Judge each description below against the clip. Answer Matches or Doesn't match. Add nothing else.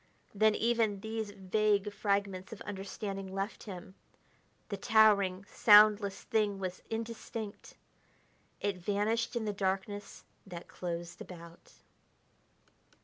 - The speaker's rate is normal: Doesn't match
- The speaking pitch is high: Matches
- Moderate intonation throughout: Doesn't match